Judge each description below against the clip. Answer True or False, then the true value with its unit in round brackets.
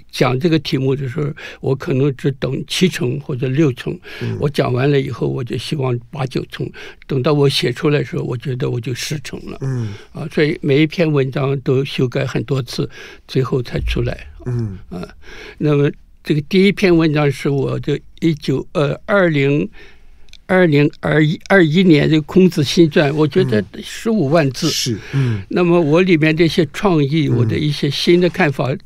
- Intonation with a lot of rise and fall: False (3.7 semitones)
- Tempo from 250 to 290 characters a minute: True (260 characters per minute)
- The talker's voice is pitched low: False (150 Hz)